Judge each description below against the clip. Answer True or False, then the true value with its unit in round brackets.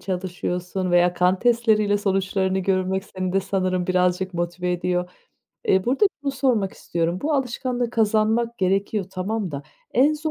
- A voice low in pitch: False (190 Hz)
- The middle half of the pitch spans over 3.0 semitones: True (3.8 semitones)